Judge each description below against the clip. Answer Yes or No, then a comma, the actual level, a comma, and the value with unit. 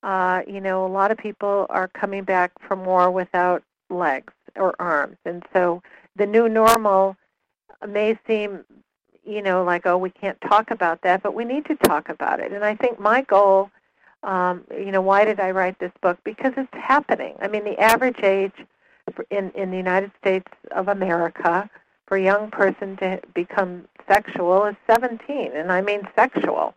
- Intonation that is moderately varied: No, narrow, 2.3 semitones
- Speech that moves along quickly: No, average, 180 wpm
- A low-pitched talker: No, high, 195 Hz